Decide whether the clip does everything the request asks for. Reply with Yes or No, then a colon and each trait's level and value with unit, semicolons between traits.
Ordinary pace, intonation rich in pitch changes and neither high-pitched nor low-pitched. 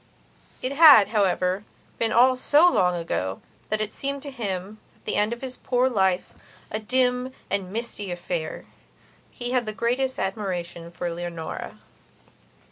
No: average, 150 wpm; wide, 5.7 semitones; high, 215 Hz